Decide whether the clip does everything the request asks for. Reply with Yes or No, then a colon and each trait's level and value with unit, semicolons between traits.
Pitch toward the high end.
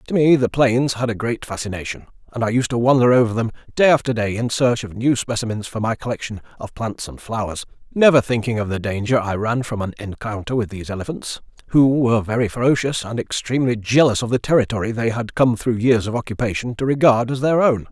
No: low, 115 Hz